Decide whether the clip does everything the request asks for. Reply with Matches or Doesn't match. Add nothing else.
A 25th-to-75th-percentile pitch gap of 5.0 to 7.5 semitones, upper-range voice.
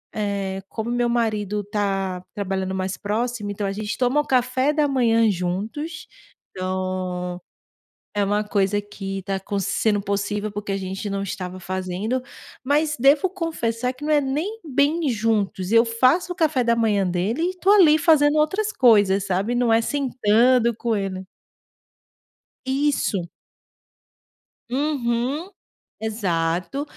Matches